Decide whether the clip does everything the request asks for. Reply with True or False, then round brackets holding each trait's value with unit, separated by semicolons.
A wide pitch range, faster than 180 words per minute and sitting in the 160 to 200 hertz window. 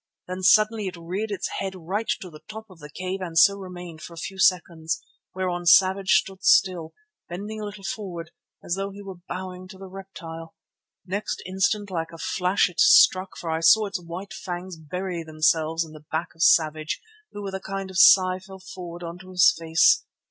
False (2.5 semitones; 200 wpm; 185 Hz)